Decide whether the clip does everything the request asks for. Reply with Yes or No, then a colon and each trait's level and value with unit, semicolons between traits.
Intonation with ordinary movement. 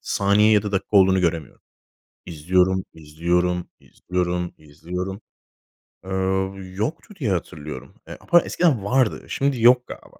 Yes: average, 3.1 semitones